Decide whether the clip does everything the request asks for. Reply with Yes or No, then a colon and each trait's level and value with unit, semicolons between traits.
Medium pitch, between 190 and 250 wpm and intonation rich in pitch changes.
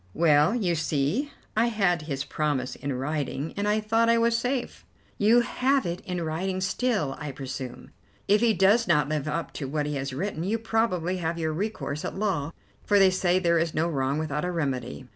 Yes: medium, 170 Hz; average, 200 wpm; wide, 6.0 semitones